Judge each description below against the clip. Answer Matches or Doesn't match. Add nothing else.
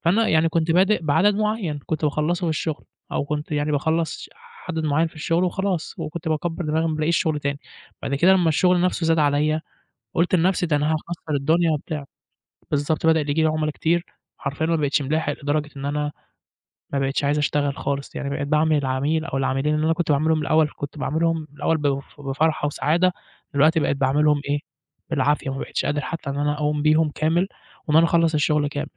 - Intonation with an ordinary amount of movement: Doesn't match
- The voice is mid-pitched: Matches